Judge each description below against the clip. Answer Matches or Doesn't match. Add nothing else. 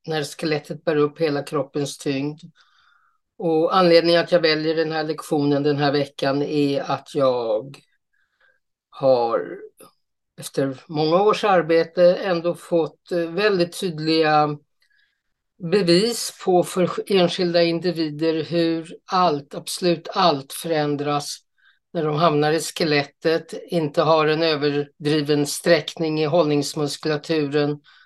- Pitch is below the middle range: Doesn't match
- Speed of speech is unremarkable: Doesn't match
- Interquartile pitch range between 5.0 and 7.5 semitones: Doesn't match